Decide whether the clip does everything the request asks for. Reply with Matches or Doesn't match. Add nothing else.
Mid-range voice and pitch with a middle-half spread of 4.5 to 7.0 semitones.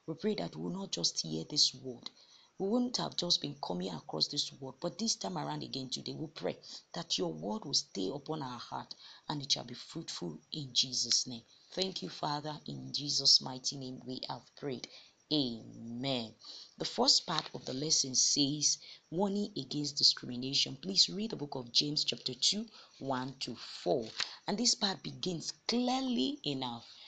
Matches